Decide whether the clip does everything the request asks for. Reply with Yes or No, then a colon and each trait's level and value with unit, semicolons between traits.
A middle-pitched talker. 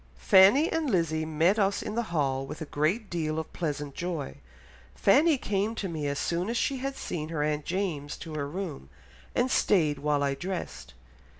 Yes: medium, 165 Hz